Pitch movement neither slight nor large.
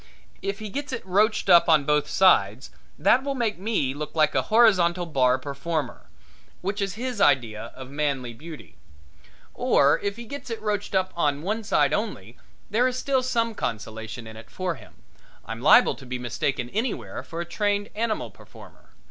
No: wide, 8.2 semitones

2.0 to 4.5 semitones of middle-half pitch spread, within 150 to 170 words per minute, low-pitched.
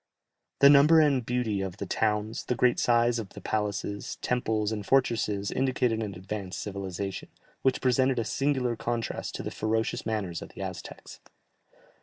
Yes: average, 3.4 semitones; average, 160 wpm; low, 110 Hz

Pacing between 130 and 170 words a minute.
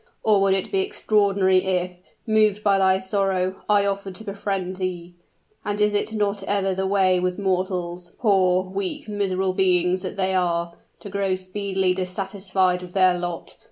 Yes: average, 165 wpm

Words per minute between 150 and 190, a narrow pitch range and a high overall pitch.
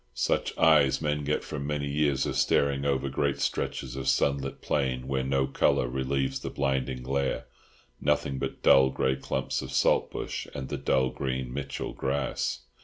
No: average, 160 wpm; narrow, 1.0 semitones; very low, 65 Hz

